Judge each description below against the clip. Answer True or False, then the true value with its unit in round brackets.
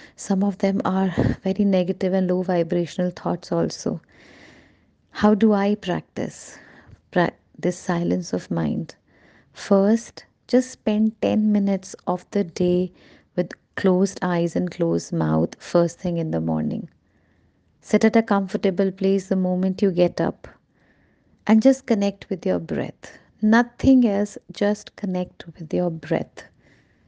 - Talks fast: False (135 wpm)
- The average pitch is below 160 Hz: False (185 Hz)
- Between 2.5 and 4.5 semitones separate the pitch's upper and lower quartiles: True (3.4 semitones)